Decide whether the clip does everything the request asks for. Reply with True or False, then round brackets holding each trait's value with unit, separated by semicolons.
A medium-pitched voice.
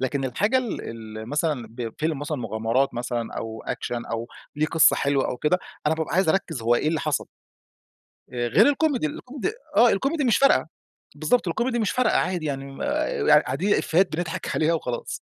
True (155 Hz)